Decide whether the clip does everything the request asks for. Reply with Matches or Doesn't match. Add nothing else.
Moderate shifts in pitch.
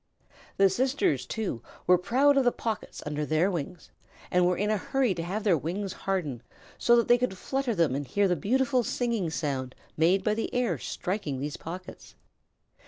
Doesn't match